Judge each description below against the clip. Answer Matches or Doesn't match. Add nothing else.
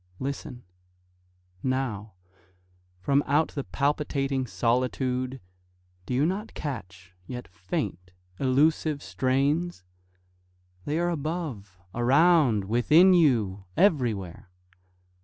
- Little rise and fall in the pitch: Doesn't match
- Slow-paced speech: Matches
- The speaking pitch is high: Doesn't match